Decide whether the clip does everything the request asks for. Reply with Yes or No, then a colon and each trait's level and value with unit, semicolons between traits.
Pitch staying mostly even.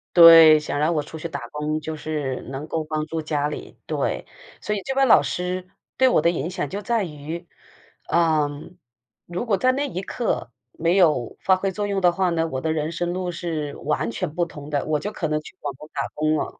No: average, 3.2 semitones